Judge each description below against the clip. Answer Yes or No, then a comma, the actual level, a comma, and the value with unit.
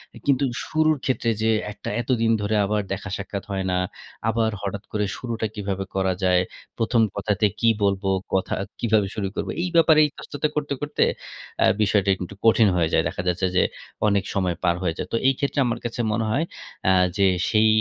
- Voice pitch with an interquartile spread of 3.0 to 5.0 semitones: Yes, average, 3.3 semitones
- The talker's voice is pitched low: Yes, low, 105 Hz